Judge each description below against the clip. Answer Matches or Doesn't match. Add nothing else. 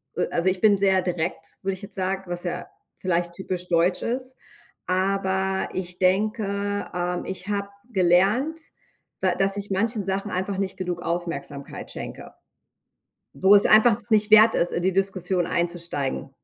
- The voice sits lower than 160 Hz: Doesn't match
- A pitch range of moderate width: Doesn't match